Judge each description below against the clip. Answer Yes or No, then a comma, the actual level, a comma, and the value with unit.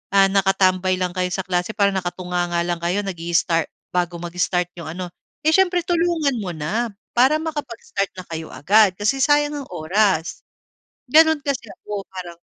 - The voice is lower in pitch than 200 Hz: Yes, high, 190 Hz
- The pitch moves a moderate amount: No, wide, 6.0 semitones